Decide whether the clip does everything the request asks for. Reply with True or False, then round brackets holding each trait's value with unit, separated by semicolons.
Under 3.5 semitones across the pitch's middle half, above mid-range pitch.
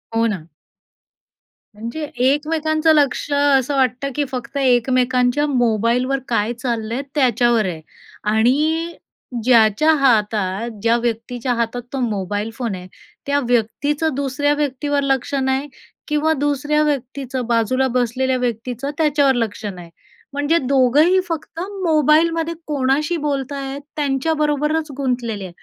False (3.8 semitones; 265 Hz)